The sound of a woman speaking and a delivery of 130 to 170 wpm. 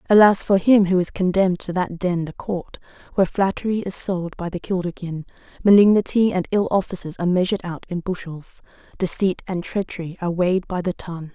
No: female; average, 185 wpm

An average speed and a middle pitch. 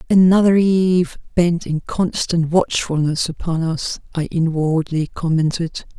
No: slow, 110 wpm; medium, 170 Hz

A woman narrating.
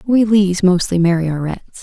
Yes: female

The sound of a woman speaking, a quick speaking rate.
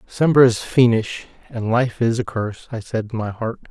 No: male; fast, 210 wpm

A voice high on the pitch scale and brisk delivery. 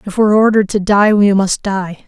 Yes: high, 200 Hz; fast, 260 wpm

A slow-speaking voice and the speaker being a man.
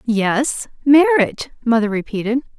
No: slow, 95 wpm; female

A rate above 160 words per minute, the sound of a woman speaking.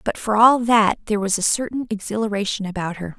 Yes: fast, 205 wpm; female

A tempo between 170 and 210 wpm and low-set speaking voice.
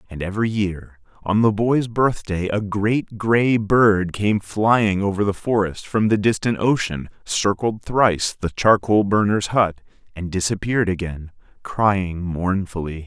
No: average, 140 wpm; low, 100 Hz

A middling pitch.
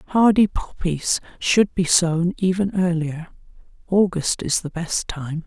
Yes: medium, 175 Hz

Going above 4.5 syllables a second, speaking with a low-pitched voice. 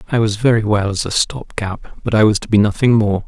Yes: 5.6 syllables/s; low, 110 Hz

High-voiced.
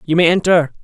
No: medium, 170 Hz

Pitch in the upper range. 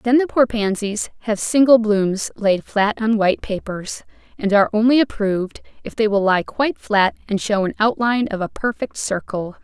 Yes: high, 215 Hz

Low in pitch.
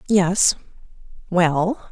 No: medium, 185 Hz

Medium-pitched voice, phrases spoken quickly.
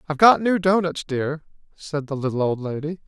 No: medium, 155 Hz; average, 195 wpm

